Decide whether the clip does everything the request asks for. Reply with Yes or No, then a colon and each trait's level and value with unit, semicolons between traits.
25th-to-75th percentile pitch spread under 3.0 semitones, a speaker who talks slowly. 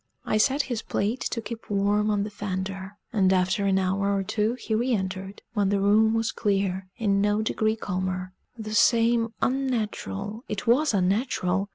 No: narrow, 2.5 semitones; average, 175 wpm